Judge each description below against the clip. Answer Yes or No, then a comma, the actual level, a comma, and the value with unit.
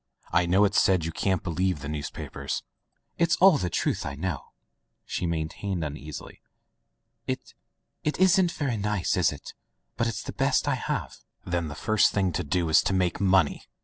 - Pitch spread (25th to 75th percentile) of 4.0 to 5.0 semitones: Yes, average, 4.4 semitones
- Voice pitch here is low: Yes, very low, 90 Hz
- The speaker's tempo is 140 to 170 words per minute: No, average, 180 wpm